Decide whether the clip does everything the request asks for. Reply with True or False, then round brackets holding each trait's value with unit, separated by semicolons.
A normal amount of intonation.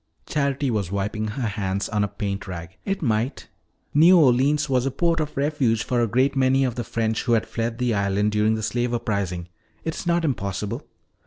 True (4.7 semitones)